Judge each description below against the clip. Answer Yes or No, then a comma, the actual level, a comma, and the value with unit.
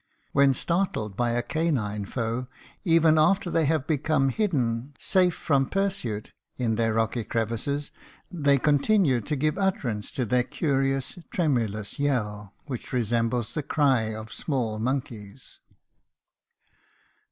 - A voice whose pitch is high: No, low, 130 Hz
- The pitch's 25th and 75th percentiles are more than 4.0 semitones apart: Yes, average, 5.2 semitones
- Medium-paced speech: No, slow, 125 wpm